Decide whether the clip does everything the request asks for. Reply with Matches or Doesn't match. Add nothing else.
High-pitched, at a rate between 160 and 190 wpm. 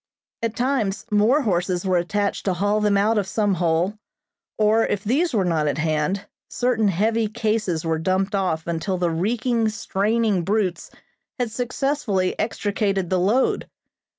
Doesn't match